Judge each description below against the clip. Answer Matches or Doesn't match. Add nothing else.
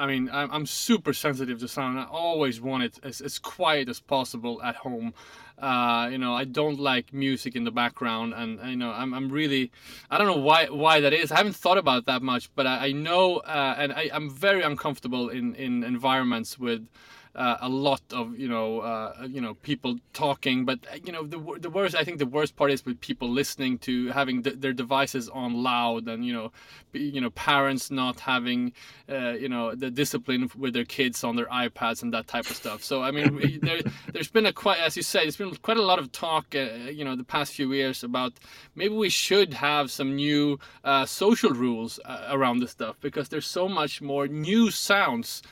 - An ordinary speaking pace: Doesn't match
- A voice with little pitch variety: Doesn't match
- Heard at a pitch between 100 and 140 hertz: Matches